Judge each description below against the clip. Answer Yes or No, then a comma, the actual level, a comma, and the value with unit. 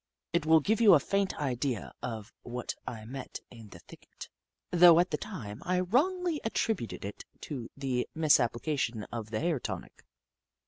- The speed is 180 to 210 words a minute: No, average, 170 wpm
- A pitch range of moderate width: No, wide, 7.4 semitones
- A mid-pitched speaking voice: Yes, medium, 145 Hz